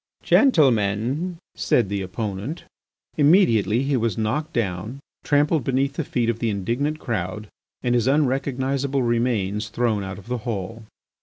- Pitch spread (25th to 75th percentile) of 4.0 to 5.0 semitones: Yes, average, 4.6 semitones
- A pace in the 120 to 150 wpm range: Yes, average, 140 wpm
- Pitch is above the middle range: No, low, 120 Hz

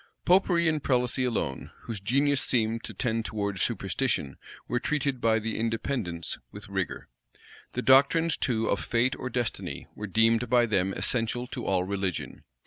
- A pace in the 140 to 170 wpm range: Yes, average, 155 wpm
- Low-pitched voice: Yes, low, 115 Hz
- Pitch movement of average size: Yes, average, 3.4 semitones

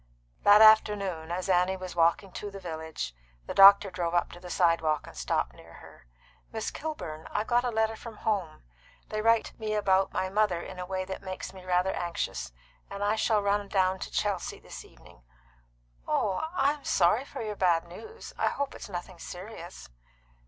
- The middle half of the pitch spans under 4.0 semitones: Yes, average, 3.3 semitones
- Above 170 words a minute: Yes, average, 185 wpm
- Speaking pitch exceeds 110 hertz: Yes, high, 190 Hz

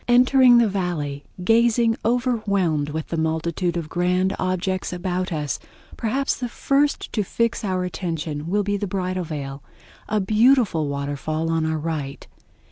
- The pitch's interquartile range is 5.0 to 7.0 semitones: Yes, wide, 5.5 semitones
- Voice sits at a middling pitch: Yes, medium, 180 Hz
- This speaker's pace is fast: No, average, 145 wpm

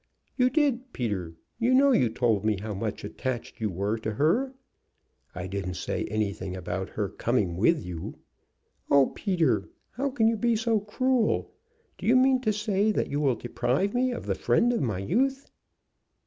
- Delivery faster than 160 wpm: Yes, average, 175 wpm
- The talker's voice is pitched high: No, medium, 145 Hz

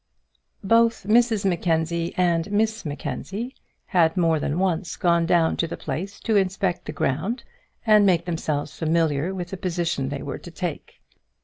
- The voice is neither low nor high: Yes, medium, 175 Hz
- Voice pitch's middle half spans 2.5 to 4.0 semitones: Yes, average, 3.3 semitones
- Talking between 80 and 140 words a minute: No, average, 155 wpm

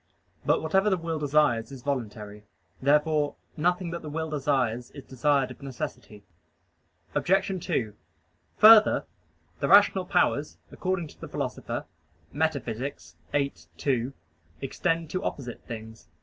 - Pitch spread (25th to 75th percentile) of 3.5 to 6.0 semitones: Yes, average, 4.9 semitones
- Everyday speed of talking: No, slow, 125 wpm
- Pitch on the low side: No, medium, 145 Hz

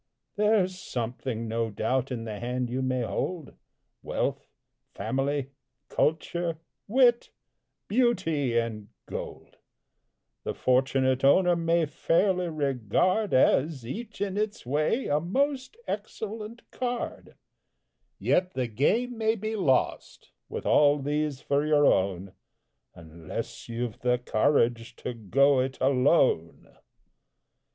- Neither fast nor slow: No, slow, 110 wpm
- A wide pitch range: Yes, wide, 7.2 semitones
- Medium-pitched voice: Yes, medium, 145 Hz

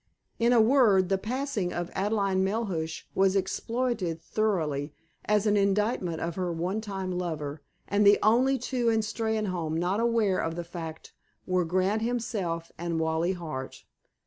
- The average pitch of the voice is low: No, high, 190 Hz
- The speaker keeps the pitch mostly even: No, average, 4.3 semitones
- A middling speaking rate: Yes, average, 150 wpm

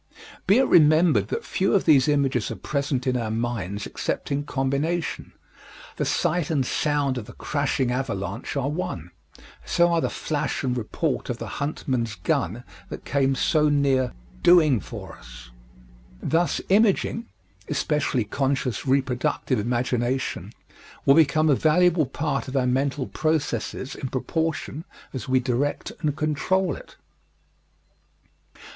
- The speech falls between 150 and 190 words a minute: No, average, 140 wpm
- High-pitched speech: No, medium, 140 Hz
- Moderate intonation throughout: Yes, average, 3.8 semitones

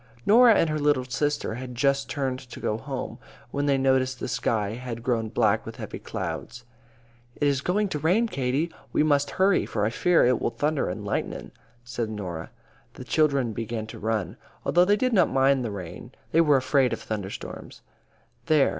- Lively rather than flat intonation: No, average, 4.5 semitones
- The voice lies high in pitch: No, low, 130 Hz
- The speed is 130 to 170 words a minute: No, average, 195 wpm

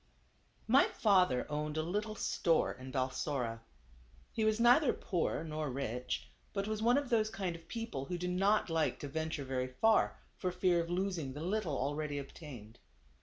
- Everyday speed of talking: Yes, average, 170 wpm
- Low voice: No, medium, 165 Hz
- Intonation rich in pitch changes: Yes, wide, 6.9 semitones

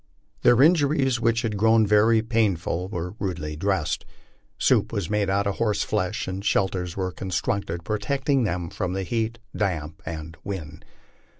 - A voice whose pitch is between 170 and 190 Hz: No, low, 100 Hz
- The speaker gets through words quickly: No, average, 155 wpm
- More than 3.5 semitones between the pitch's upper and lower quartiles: Yes, average, 4.0 semitones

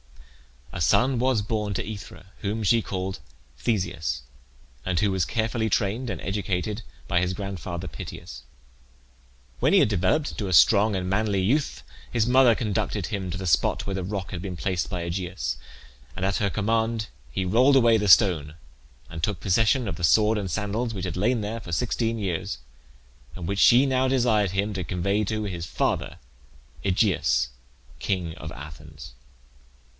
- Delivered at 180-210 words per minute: No, average, 170 wpm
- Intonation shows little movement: No, average, 3.6 semitones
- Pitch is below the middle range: Yes, low, 100 Hz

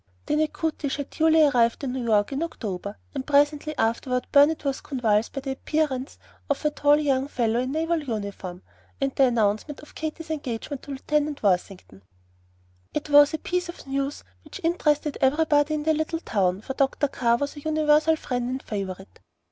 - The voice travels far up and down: No, average, 4.1 semitones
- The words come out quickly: No, average, 180 wpm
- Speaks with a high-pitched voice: Yes, very high, 280 Hz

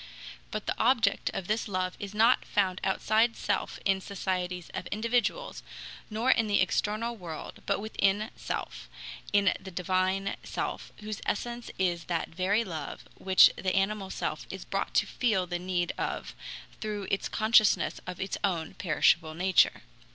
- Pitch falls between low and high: No, high, 195 Hz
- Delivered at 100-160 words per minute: Yes, average, 155 wpm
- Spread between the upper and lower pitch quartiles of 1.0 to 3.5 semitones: Yes, average, 2.8 semitones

